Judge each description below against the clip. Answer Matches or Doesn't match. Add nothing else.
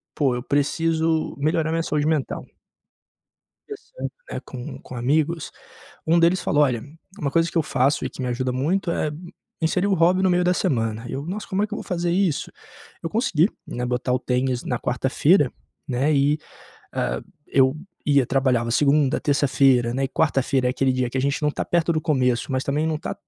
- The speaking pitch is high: Doesn't match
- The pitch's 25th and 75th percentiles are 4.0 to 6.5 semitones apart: Matches